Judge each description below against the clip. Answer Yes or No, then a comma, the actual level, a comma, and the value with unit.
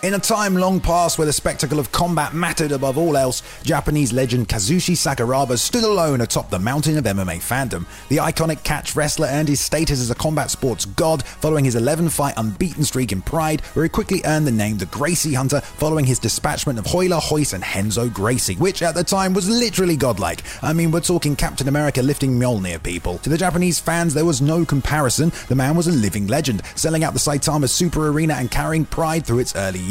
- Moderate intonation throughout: Yes, average, 4.8 semitones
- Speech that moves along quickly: Yes, fast, 215 wpm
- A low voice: No, medium, 150 Hz